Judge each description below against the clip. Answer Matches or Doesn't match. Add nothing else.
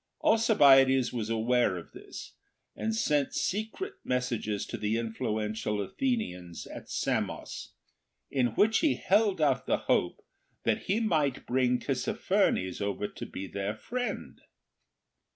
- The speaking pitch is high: Doesn't match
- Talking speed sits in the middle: Doesn't match